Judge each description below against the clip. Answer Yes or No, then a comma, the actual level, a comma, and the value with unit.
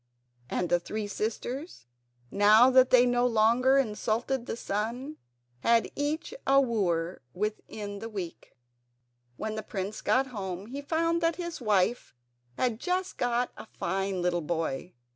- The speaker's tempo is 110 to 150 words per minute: Yes, average, 140 wpm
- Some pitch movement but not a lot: Yes, average, 4.7 semitones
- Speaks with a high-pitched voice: Yes, high, 225 Hz